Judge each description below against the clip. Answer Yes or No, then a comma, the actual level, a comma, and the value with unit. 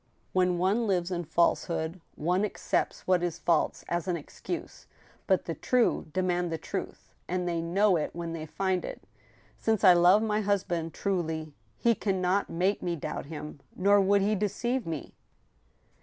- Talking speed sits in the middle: Yes, average, 170 wpm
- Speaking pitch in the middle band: Yes, medium, 180 Hz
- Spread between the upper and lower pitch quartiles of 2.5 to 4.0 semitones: Yes, average, 3.0 semitones